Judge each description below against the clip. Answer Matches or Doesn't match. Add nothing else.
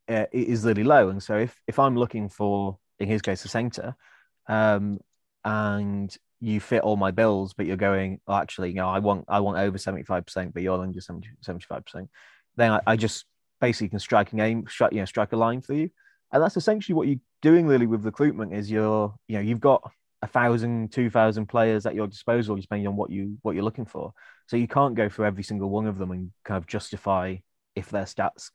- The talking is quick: Matches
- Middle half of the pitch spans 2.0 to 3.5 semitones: Matches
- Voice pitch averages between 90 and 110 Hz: Matches